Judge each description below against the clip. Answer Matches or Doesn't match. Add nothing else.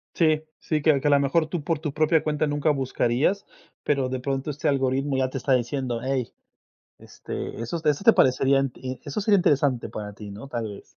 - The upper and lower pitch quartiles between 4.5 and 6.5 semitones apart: Doesn't match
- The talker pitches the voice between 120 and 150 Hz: Matches